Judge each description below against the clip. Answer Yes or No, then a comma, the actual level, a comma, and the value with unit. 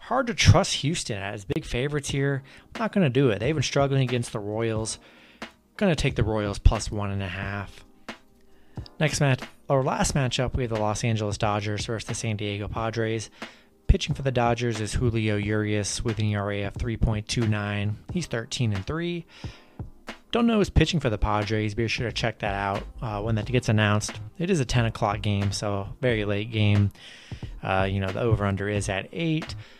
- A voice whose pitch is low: Yes, low, 115 Hz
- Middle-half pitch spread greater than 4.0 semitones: Yes, average, 4.5 semitones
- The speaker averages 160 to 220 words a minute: Yes, average, 195 wpm